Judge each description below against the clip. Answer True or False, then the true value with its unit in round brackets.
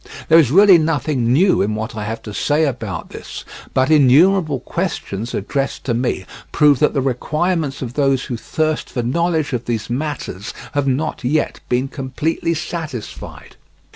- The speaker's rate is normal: True (165 wpm)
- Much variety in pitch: False (4.4 semitones)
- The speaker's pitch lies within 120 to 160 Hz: True (135 Hz)